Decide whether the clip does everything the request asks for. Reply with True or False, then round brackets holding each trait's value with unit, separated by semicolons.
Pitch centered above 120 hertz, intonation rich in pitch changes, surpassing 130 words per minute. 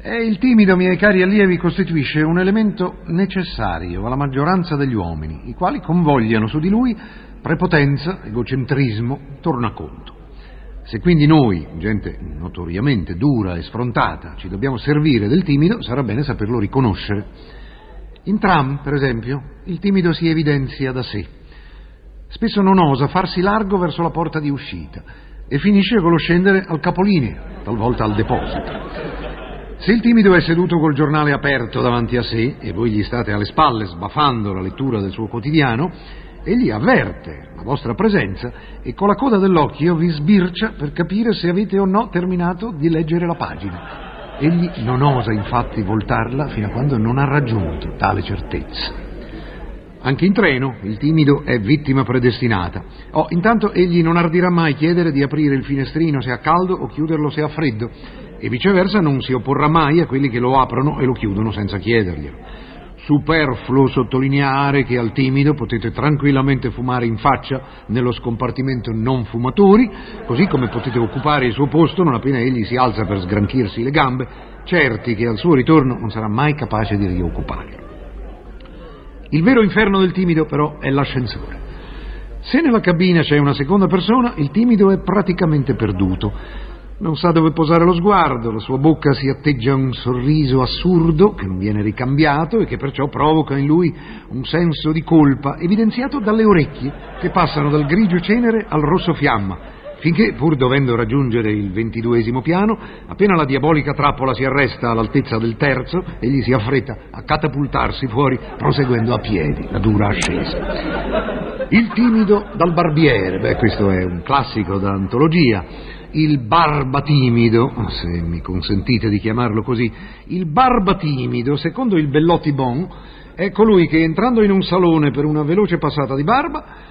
True (140 Hz; 6.3 semitones; 160 wpm)